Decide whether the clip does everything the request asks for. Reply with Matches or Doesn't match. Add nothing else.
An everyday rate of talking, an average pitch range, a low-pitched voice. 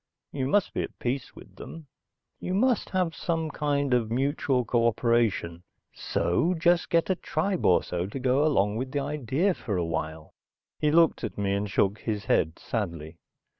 Doesn't match